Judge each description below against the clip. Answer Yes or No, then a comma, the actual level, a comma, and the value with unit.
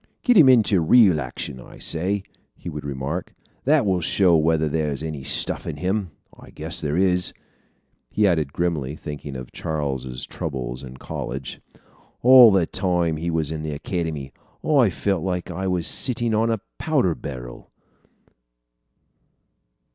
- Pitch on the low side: Yes, very low, 80 Hz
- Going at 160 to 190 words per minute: No, average, 150 wpm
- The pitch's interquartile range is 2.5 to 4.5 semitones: No, average, 5.0 semitones